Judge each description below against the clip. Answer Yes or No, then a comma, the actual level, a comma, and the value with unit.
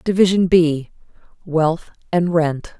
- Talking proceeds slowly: Yes, slow, 85 wpm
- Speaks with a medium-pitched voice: Yes, medium, 170 Hz